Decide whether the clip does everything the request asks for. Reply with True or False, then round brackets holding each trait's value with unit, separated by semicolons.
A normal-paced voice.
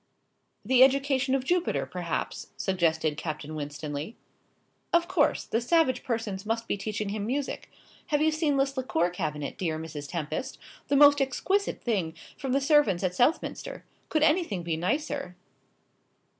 True (145 wpm)